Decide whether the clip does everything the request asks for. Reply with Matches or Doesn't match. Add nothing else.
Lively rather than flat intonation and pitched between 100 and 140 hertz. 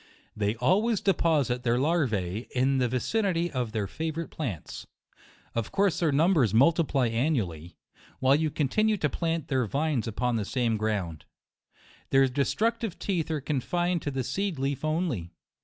Matches